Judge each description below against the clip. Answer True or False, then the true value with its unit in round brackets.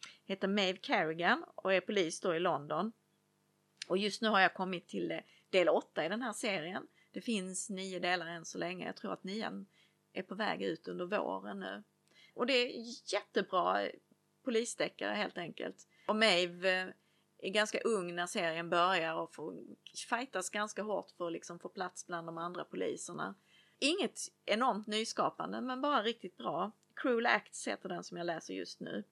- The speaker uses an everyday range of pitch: True (3.8 semitones)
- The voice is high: True (195 Hz)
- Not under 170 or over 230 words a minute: True (175 wpm)